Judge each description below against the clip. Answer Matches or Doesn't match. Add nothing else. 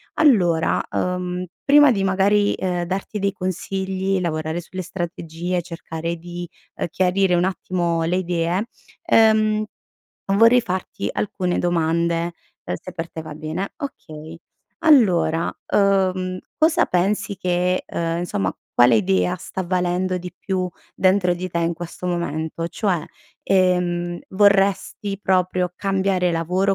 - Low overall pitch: Doesn't match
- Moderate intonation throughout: Doesn't match